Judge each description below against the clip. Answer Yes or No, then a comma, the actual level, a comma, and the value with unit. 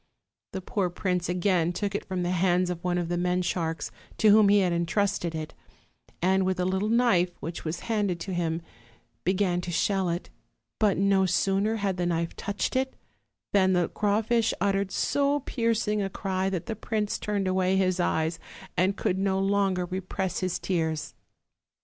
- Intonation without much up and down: Yes, narrow, 2.3 semitones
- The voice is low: No, high, 190 Hz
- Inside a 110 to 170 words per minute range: No, average, 180 wpm